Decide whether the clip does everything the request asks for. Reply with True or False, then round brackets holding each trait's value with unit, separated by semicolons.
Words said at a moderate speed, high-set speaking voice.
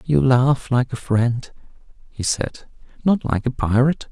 False (145 wpm; 125 Hz)